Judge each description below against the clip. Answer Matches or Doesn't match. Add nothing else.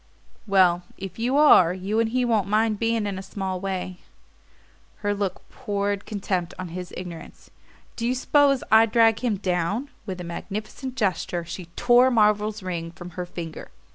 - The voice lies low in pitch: Doesn't match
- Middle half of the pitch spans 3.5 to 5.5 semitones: Matches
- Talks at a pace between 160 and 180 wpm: Matches